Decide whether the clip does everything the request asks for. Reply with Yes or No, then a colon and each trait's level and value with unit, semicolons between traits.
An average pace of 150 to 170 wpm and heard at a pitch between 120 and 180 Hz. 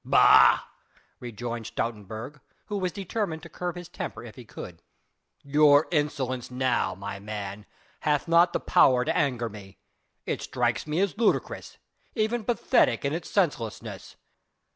No: average, 140 wpm; low, 135 Hz